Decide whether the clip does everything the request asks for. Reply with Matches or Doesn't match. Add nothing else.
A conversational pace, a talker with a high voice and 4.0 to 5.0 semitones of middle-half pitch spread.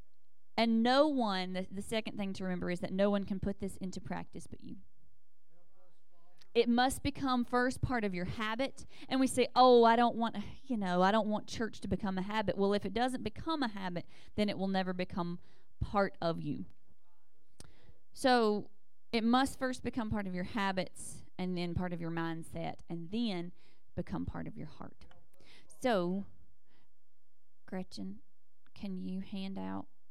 Matches